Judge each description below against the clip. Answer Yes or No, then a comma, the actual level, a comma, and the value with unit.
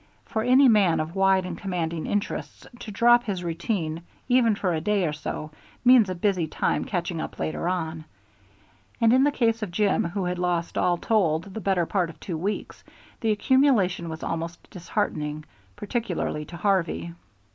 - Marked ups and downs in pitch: No, average, 4.2 semitones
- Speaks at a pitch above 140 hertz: Yes, medium, 185 Hz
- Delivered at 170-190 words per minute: Yes, average, 175 wpm